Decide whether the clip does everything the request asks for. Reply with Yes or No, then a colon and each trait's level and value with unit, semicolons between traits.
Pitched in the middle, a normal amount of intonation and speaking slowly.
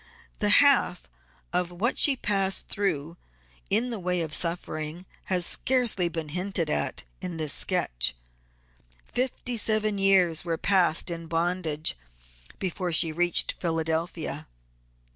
Yes: medium, 175 Hz; average, 3.2 semitones; slow, 125 wpm